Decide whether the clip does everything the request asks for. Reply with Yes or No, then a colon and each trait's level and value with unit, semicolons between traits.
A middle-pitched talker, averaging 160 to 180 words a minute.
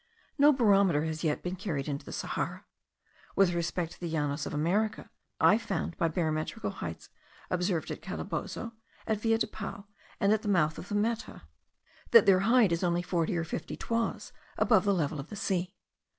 No: medium, 180 Hz; average, 190 wpm